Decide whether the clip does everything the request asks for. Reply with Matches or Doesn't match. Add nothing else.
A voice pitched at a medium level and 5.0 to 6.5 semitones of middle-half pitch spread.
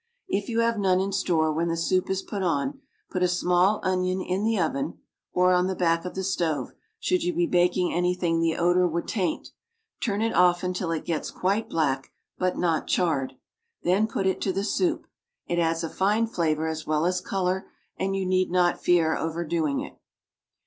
Doesn't match